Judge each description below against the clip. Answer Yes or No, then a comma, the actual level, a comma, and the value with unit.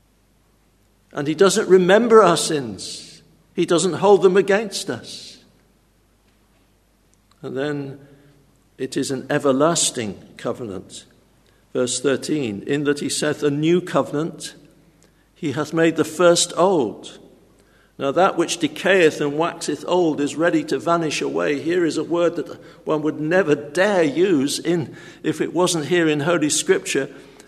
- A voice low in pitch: No, medium, 155 Hz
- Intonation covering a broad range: No, average, 3.6 semitones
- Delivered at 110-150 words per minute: Yes, average, 140 wpm